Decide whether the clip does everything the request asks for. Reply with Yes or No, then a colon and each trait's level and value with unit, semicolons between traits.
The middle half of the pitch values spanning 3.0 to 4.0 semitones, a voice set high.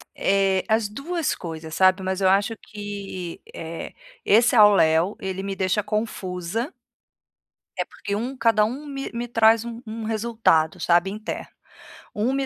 Yes: average, 3.4 semitones; high, 210 Hz